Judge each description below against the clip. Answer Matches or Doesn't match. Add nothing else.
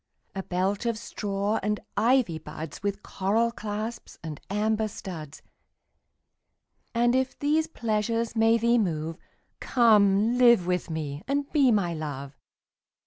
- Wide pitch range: Doesn't match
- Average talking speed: Doesn't match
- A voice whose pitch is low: Doesn't match